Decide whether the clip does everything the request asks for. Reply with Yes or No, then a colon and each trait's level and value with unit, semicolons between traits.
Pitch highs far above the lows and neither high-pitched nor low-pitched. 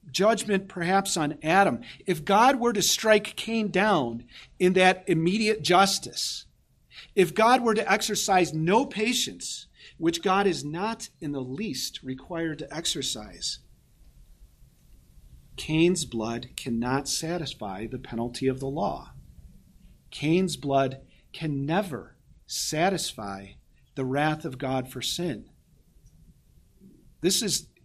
Yes: wide, 7.0 semitones; medium, 160 Hz